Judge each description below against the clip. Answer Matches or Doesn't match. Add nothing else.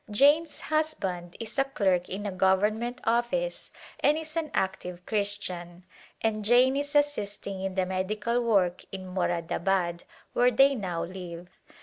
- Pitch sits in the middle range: Doesn't match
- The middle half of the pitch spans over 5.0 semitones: Matches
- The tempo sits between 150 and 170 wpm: Doesn't match